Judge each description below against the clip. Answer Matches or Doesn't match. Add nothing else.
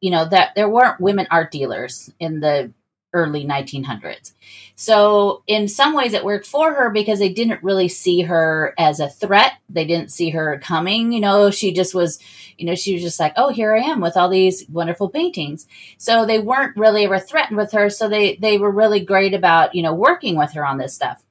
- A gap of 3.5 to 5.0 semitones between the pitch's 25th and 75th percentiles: Matches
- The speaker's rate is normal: Doesn't match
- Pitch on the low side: Doesn't match